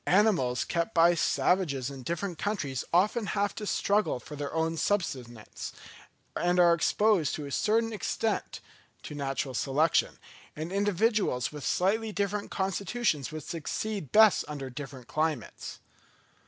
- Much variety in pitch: Yes, wide, 6.2 semitones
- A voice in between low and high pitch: Yes, medium, 170 Hz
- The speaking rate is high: No, slow, 135 wpm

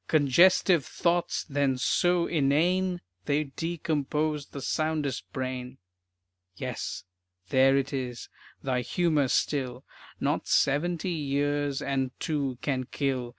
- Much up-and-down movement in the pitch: No, average, 3.1 semitones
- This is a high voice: No, medium, 145 Hz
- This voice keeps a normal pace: No, slow, 110 wpm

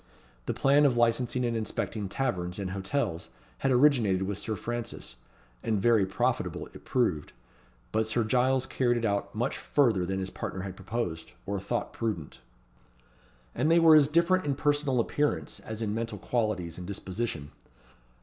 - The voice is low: Yes, low, 115 Hz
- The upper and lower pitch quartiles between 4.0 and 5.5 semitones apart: Yes, average, 5.2 semitones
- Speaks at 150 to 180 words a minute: Yes, average, 160 wpm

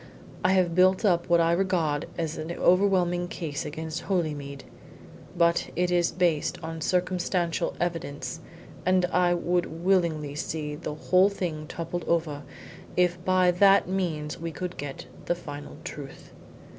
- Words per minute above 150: No, average, 145 wpm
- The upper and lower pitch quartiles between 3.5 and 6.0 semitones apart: No, narrow, 2.5 semitones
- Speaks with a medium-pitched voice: Yes, medium, 170 Hz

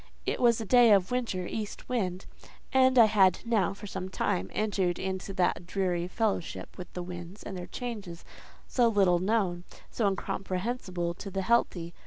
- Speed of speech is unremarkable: Yes, average, 170 wpm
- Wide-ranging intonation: No, average, 3.8 semitones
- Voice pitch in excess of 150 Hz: Yes, high, 190 Hz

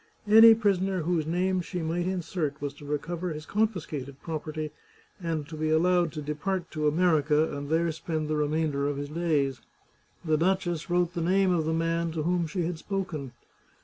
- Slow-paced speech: No, average, 180 wpm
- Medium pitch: Yes, medium, 165 Hz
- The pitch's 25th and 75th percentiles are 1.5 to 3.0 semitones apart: Yes, average, 2.7 semitones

